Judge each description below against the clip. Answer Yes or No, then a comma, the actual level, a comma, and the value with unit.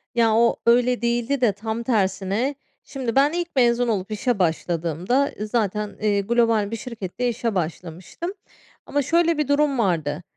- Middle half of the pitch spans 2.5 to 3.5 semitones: No, average, 4.0 semitones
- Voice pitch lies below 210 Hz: No, high, 230 Hz